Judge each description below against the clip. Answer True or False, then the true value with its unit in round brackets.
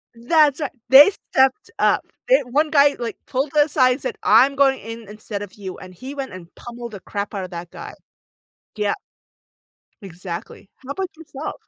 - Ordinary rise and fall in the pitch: False (5.9 semitones)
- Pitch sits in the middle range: False (255 Hz)